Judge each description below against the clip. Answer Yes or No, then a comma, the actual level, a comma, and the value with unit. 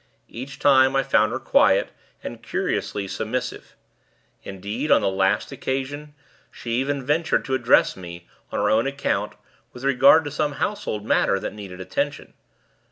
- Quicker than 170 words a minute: No, average, 155 wpm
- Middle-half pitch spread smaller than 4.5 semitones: No, average, 5.3 semitones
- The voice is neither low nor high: No, low, 130 Hz